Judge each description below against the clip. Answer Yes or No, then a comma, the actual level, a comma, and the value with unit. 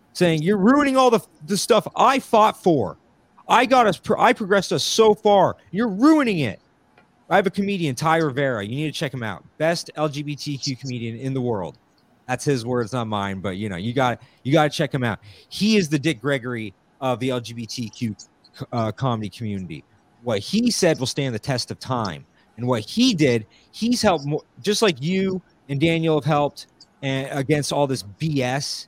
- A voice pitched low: No, medium, 145 Hz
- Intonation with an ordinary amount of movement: No, wide, 7.2 semitones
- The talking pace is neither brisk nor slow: Yes, average, 195 wpm